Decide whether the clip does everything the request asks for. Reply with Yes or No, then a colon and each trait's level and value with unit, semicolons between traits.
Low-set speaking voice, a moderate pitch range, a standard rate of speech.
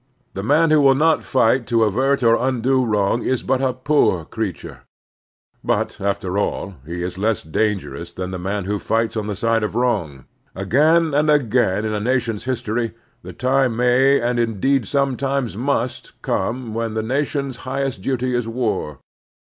Yes: low, 115 Hz; average, 4.3 semitones; average, 170 wpm